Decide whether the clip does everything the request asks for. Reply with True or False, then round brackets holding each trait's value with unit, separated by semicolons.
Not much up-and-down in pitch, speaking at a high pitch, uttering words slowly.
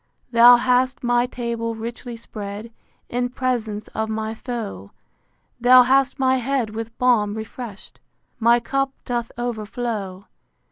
True (2.2 semitones; 235 Hz; 125 wpm)